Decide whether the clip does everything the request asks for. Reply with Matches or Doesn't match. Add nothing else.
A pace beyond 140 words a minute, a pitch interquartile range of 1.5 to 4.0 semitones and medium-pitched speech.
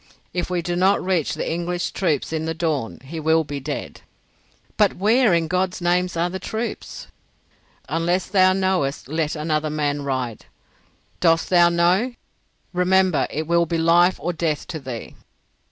Matches